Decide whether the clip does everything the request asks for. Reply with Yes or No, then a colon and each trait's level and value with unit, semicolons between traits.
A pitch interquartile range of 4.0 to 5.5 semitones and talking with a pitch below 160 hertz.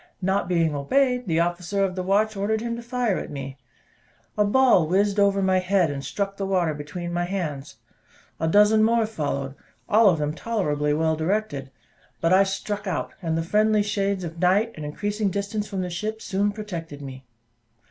No: average, 4.4 semitones; high, 190 Hz